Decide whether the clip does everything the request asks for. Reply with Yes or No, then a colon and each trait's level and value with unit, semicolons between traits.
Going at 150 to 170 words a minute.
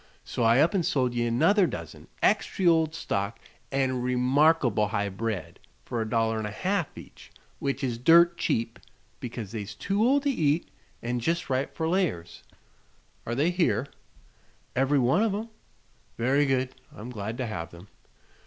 Yes: average, 165 wpm